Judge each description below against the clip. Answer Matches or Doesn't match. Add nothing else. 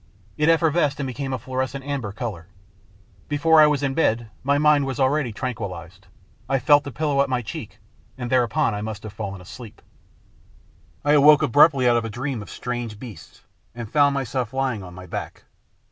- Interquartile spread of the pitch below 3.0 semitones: Doesn't match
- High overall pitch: Doesn't match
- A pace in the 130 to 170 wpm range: Doesn't match